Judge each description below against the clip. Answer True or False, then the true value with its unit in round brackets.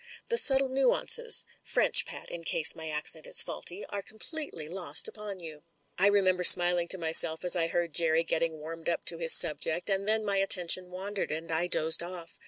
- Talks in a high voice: False (175 Hz)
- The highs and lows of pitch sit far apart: False (3.3 semitones)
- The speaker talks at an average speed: True (195 wpm)